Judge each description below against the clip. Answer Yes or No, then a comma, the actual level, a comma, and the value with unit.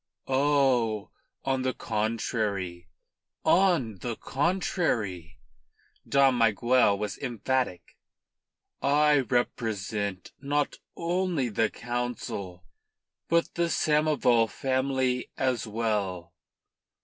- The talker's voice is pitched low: Yes, low, 120 Hz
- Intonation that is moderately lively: Yes, average, 4.7 semitones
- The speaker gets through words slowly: Yes, slow, 80 wpm